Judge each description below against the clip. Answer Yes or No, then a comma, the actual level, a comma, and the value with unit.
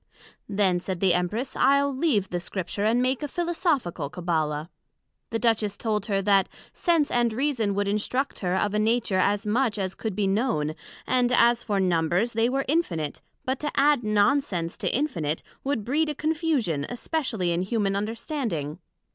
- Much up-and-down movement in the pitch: Yes, wide, 5.8 semitones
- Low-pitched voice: No, high, 215 Hz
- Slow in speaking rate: No, average, 170 wpm